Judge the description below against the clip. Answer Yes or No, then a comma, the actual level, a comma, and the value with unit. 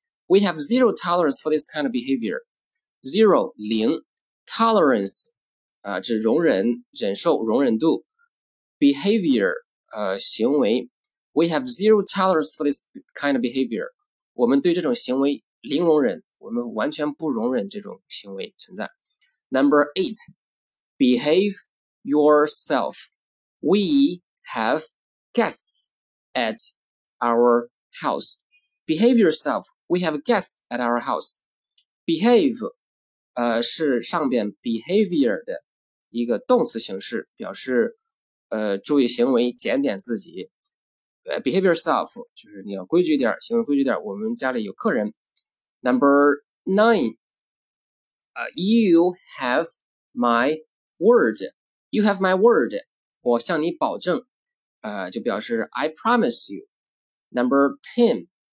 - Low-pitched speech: No, high, 210 Hz